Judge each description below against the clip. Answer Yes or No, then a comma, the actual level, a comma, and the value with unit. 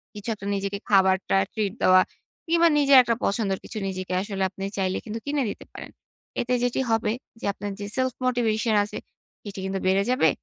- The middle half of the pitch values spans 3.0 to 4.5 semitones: Yes, average, 3.7 semitones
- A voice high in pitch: Yes, high, 205 Hz